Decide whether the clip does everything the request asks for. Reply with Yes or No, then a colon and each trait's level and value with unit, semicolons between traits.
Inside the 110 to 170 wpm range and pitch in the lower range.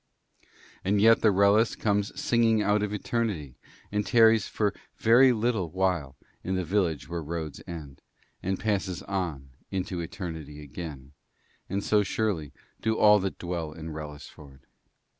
Yes: average, 145 wpm; very low, 95 Hz